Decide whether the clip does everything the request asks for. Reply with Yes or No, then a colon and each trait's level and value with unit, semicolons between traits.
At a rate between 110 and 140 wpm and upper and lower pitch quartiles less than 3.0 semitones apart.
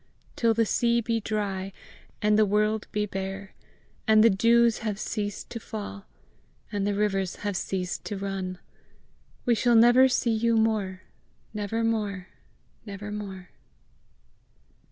Yes: slow, 135 wpm; narrow, 2.5 semitones